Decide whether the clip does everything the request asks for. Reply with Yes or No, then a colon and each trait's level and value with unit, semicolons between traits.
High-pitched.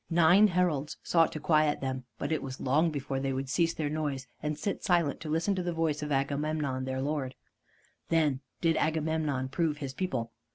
No: medium, 150 Hz